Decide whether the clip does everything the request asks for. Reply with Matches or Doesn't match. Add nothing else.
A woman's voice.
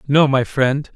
Doesn't match